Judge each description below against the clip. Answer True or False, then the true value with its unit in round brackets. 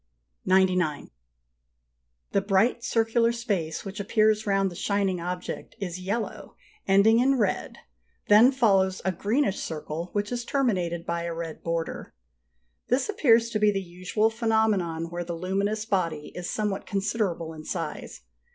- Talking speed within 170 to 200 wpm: False (150 wpm)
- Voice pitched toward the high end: True (195 Hz)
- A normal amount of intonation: True (4.2 semitones)